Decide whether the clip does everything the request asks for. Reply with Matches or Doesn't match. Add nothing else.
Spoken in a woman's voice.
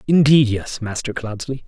Doesn't match